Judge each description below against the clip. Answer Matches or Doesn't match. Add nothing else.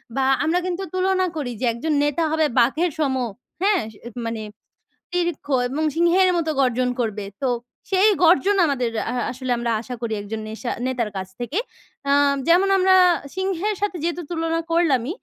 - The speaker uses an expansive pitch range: Matches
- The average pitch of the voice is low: Doesn't match